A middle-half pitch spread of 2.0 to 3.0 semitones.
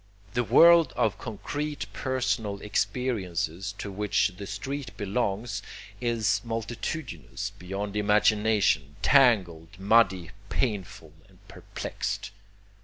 No: average, 3.8 semitones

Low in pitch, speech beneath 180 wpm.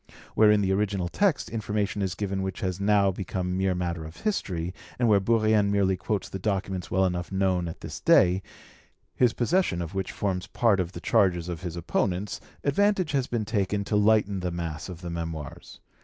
No: very low, 95 Hz; average, 195 wpm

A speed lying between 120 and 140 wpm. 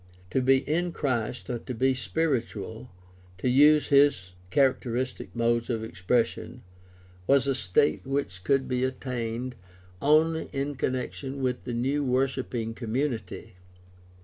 Yes: slow, 135 wpm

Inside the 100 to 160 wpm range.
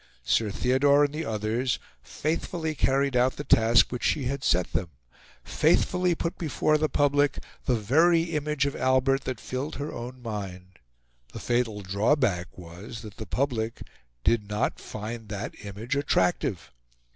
Yes: average, 150 wpm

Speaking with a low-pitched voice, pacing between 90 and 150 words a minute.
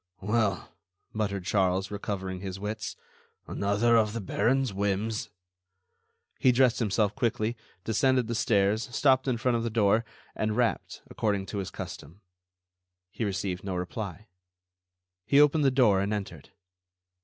Yes: low, 105 Hz; average, 140 wpm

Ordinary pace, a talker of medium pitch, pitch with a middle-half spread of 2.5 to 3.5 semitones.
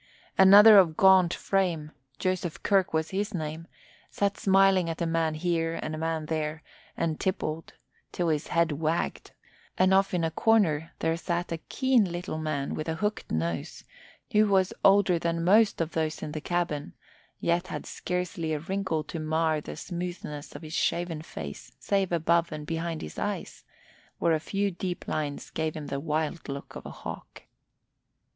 Yes: average, 170 wpm; medium, 165 Hz; average, 2.9 semitones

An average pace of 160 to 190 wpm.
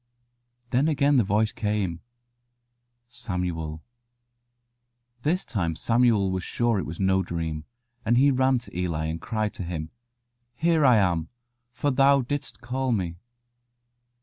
No: slow, 135 wpm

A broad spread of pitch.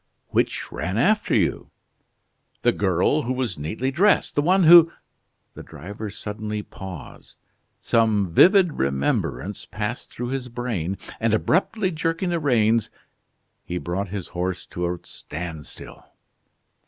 Yes: wide, 8.0 semitones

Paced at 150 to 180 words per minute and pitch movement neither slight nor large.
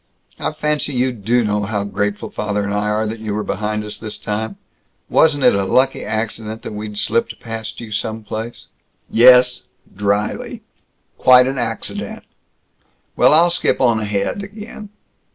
Yes: average, 160 wpm; average, 3.2 semitones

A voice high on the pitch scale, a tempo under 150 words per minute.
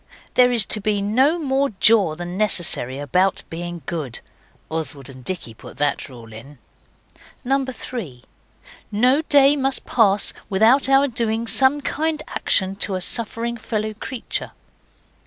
Yes: high, 215 Hz; average, 140 wpm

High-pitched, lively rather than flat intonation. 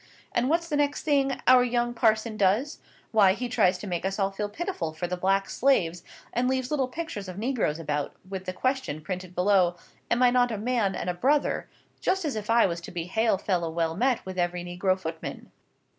Yes: high, 205 Hz; wide, 5.8 semitones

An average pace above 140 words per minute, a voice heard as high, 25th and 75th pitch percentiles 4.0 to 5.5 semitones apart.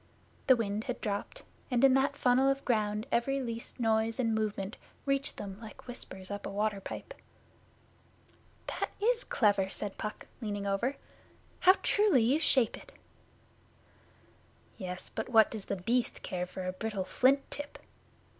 Yes: average, 155 wpm; high, 225 Hz; average, 4.4 semitones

